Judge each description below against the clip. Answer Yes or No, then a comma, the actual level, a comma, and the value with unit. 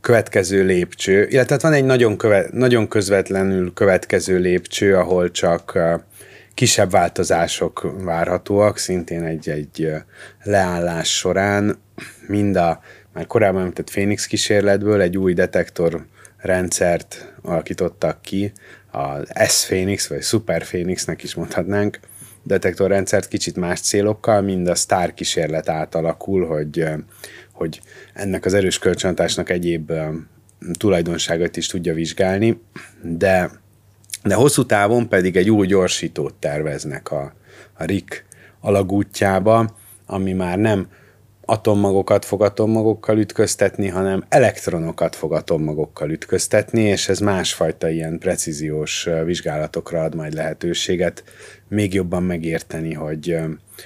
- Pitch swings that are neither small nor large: Yes, average, 3.5 semitones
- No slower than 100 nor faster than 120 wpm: Yes, average, 115 wpm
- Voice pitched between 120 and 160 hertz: No, very low, 95 Hz